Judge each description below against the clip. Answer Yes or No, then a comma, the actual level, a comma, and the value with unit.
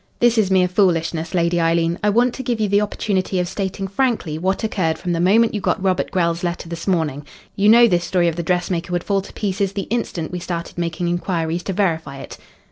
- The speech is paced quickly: Yes, fast, 225 wpm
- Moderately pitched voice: Yes, medium, 180 Hz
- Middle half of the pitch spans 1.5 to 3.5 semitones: Yes, average, 2.9 semitones